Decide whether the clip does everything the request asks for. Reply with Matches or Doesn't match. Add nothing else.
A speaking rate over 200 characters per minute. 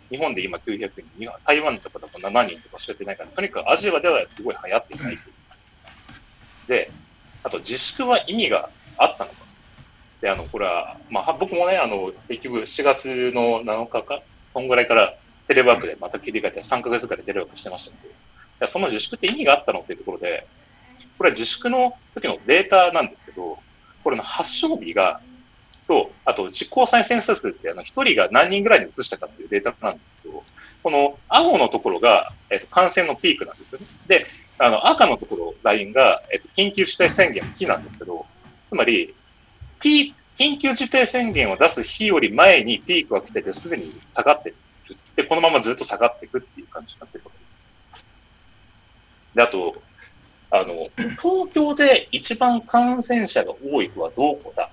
Matches